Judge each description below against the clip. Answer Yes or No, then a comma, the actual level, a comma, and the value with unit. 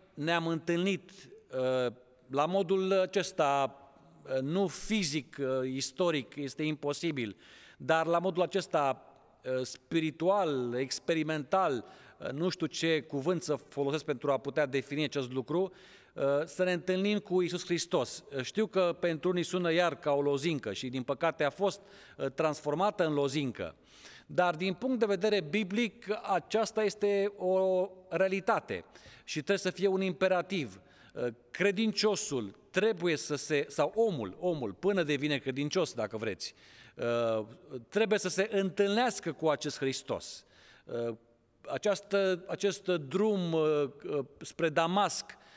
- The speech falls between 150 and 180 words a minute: No, average, 120 wpm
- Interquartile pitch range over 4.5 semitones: Yes, average, 5.3 semitones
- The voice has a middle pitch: Yes, medium, 165 Hz